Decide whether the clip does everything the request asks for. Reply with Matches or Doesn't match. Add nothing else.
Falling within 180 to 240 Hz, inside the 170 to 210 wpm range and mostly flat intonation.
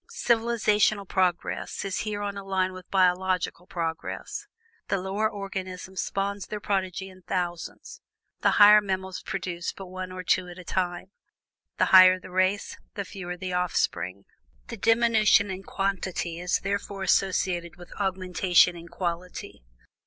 Doesn't match